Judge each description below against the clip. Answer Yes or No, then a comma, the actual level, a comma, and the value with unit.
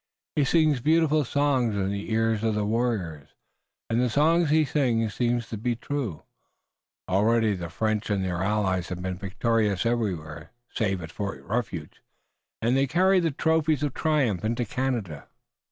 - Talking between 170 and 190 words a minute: No, average, 160 wpm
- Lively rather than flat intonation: Yes, wide, 5.8 semitones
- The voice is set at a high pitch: No, low, 115 Hz